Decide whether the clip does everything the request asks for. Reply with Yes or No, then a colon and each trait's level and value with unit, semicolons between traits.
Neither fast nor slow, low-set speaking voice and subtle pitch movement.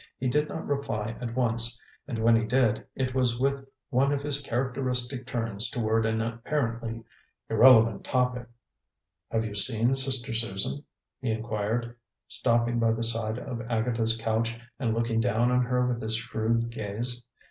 Yes: average, 160 wpm; low, 115 Hz; narrow, 1.9 semitones